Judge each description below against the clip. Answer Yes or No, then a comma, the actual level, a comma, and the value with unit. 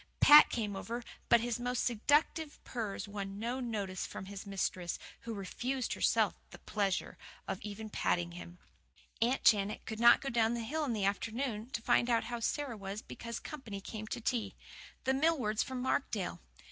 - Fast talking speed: No, average, 175 wpm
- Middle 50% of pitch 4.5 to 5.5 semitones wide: No, average, 3.6 semitones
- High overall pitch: Yes, high, 225 Hz